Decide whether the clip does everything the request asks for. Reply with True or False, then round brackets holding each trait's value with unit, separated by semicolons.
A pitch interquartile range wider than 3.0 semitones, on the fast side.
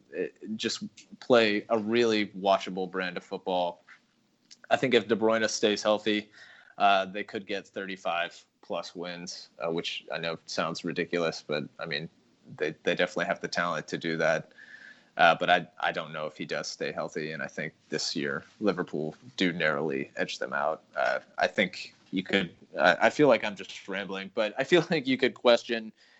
False (4.1 semitones; 185 wpm)